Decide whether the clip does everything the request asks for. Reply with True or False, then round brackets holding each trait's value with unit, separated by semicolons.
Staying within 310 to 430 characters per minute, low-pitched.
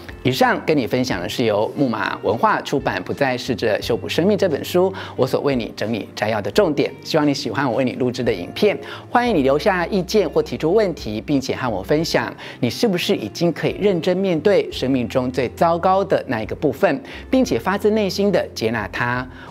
False (315 characters per minute; 170 Hz)